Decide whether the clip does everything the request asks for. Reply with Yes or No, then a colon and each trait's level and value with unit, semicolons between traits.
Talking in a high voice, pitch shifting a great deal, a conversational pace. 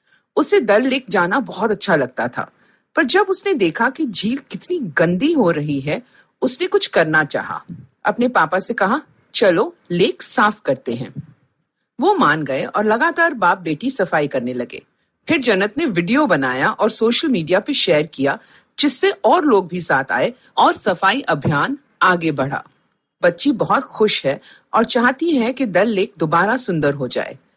Yes: high, 215 Hz; wide, 7.9 semitones; average, 170 wpm